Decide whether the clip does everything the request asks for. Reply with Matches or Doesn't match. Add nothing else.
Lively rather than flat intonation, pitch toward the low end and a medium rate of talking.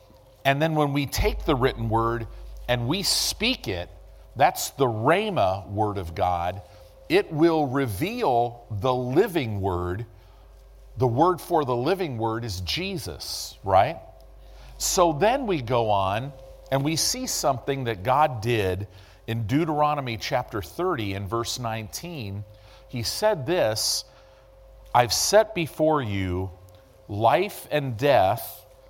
Doesn't match